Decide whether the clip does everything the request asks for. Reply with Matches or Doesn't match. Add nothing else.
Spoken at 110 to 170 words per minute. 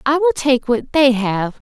Doesn't match